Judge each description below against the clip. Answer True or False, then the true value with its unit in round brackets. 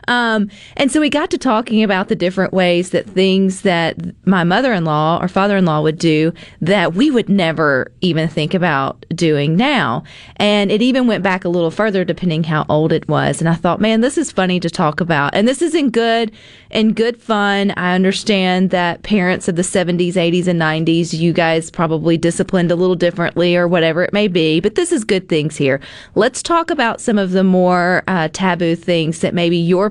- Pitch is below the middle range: False (180 Hz)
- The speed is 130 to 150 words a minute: False (200 wpm)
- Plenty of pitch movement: False (3.7 semitones)